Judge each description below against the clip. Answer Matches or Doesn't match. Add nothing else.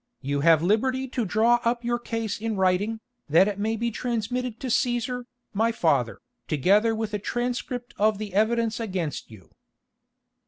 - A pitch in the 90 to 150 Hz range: Doesn't match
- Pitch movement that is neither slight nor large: Matches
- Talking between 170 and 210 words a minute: Doesn't match